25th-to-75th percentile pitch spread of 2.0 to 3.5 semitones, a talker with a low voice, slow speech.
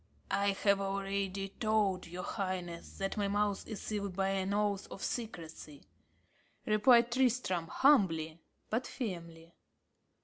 No: average, 2.7 semitones; high, 195 Hz; slow, 125 wpm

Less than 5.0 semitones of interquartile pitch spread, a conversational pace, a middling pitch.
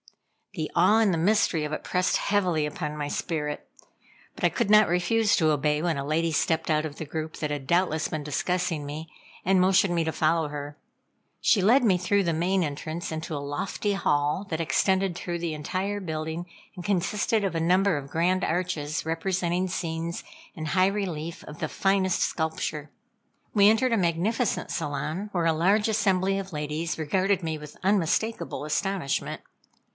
Yes: average, 3.7 semitones; average, 180 wpm; medium, 170 Hz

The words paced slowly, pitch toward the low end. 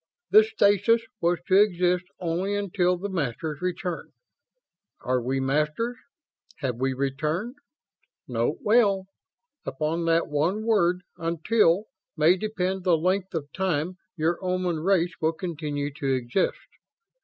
No: slow, 125 wpm; medium, 175 Hz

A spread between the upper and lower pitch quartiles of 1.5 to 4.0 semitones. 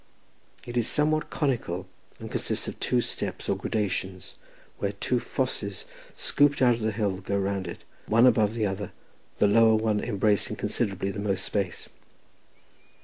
Yes: average, 3.2 semitones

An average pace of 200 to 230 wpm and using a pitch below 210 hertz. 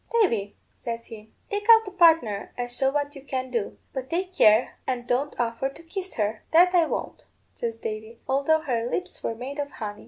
No: fast, 205 wpm; very high, 265 Hz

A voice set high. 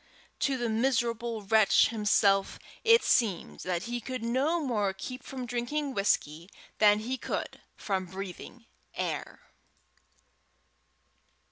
Yes: high, 230 Hz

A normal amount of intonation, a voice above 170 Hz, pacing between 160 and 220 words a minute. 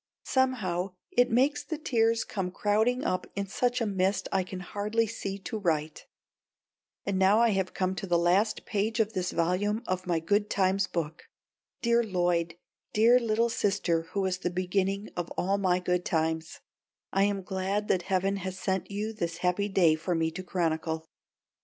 Yes: average, 3.0 semitones; high, 190 Hz; average, 180 wpm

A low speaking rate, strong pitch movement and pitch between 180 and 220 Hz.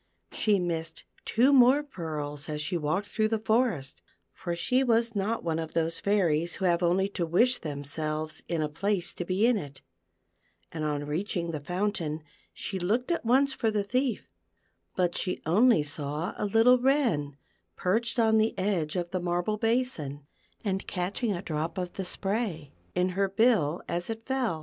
No: average, 175 wpm; wide, 5.8 semitones; medium, 185 Hz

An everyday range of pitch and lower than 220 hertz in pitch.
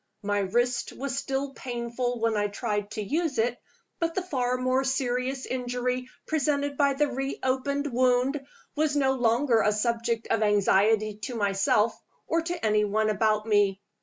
No: average, 3.9 semitones; high, 245 Hz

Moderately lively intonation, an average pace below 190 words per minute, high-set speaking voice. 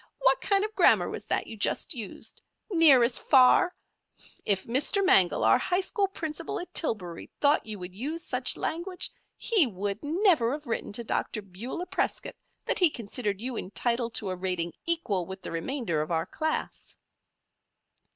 No: wide, 8.9 semitones; average, 170 wpm; high, 245 Hz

